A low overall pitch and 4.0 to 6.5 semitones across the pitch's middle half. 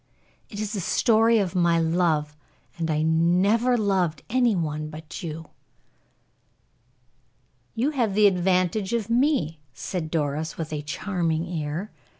No: medium, 175 Hz; average, 5.0 semitones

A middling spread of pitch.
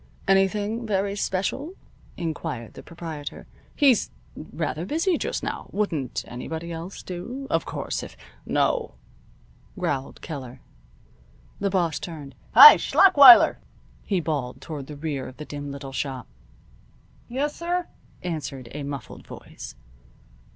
No: wide, 6.3 semitones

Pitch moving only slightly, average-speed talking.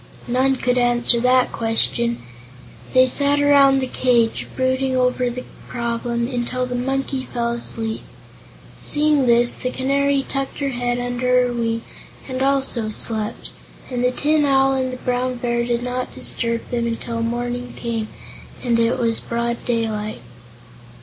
Yes: narrow, 1.7 semitones; average, 150 wpm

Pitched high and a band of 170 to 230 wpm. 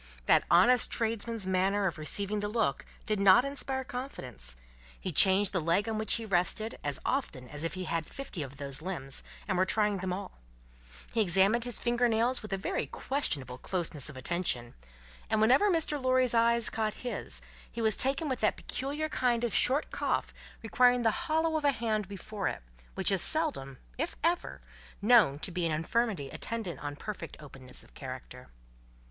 Yes: high, 210 Hz; average, 180 wpm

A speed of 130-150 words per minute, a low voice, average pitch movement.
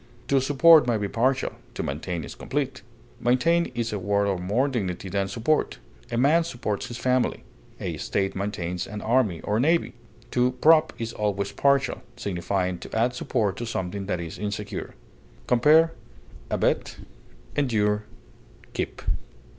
Yes: average, 145 wpm; low, 110 Hz; average, 4.9 semitones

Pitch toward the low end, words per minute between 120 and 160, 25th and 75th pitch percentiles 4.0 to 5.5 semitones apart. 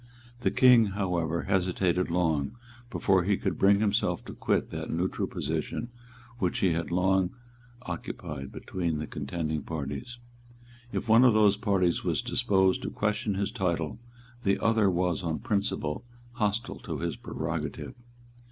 No: very low, 95 Hz; average, 145 wpm; average, 3.6 semitones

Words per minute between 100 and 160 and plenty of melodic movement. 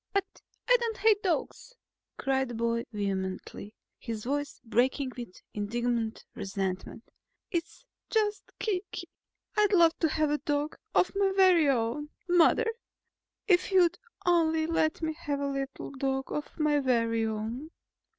Yes: average, 140 wpm; wide, 7.0 semitones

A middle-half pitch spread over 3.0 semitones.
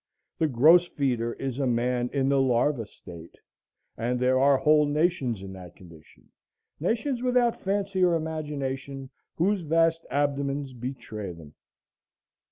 Yes: average, 5.0 semitones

